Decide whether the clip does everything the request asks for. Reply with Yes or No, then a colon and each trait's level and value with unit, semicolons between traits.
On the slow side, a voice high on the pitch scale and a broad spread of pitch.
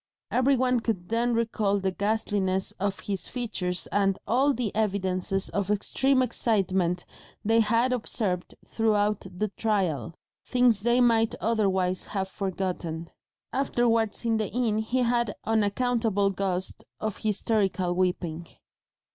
No: slow, 130 wpm; high, 210 Hz; average, 3.4 semitones